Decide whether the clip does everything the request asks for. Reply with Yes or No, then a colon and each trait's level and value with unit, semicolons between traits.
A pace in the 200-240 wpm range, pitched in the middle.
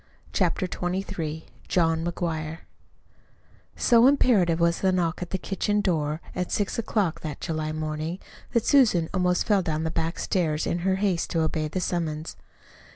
No: average, 155 wpm; medium, 170 Hz